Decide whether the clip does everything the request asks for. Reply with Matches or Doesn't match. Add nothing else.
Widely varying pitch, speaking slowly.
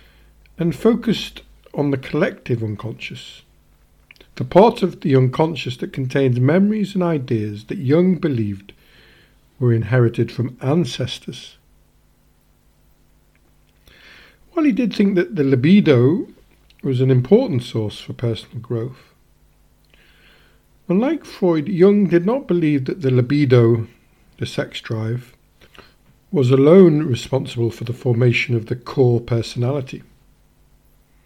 Matches